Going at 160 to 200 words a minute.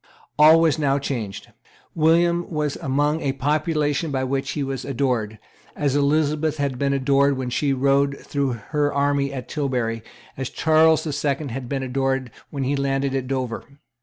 Yes: average, 165 wpm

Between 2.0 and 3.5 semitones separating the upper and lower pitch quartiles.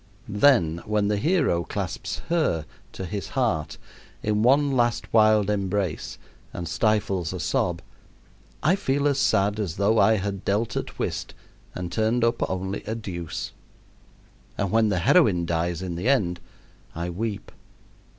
No: average, 4.4 semitones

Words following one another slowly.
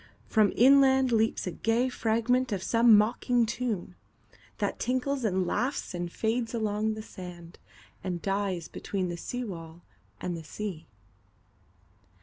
Yes: slow, 120 wpm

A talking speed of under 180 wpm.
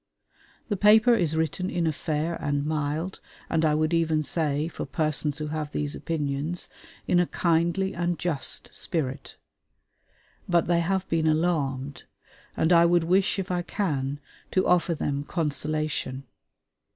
Yes: average, 150 wpm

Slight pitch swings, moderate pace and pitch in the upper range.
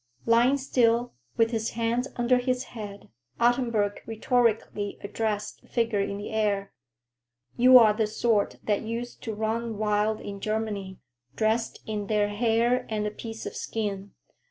Yes: narrow, 2.2 semitones; average, 150 wpm; high, 220 Hz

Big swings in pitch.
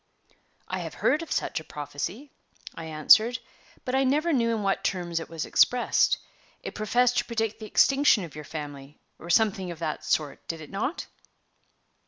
Yes: wide, 7.6 semitones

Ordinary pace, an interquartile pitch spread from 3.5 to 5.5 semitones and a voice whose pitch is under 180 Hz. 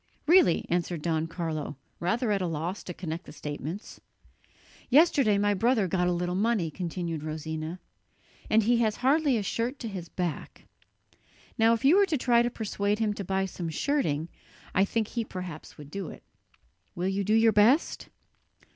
No: average, 175 wpm; average, 5.2 semitones; high, 195 Hz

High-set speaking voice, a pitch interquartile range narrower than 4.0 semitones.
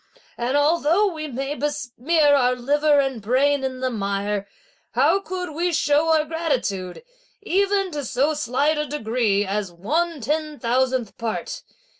No: very high, 285 Hz; average, 4.5 semitones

